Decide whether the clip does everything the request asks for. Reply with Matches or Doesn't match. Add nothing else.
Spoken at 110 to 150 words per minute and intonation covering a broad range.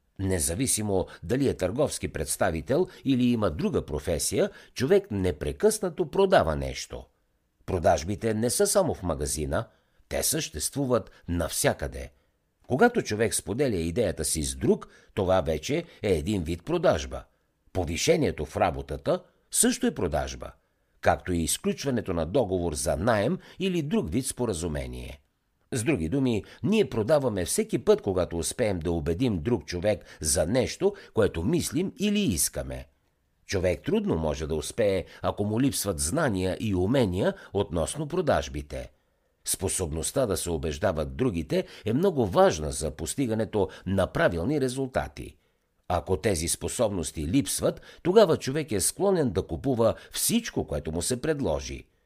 Matches